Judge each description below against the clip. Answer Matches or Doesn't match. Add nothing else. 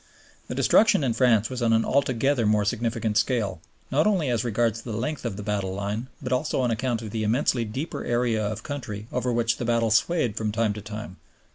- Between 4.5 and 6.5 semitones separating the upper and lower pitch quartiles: Doesn't match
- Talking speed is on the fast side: Matches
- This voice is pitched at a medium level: Doesn't match